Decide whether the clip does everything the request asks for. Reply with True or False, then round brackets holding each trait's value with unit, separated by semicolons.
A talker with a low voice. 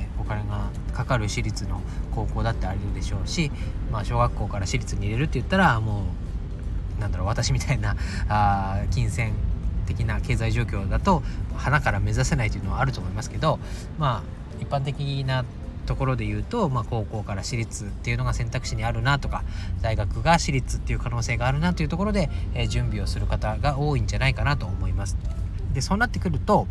True (105 Hz)